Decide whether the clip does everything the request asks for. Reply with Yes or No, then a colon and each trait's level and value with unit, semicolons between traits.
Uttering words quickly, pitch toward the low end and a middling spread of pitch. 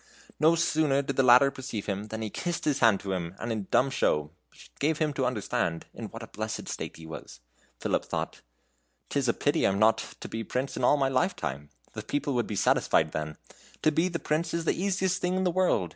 No: fast, 235 wpm; low, 130 Hz; wide, 6.8 semitones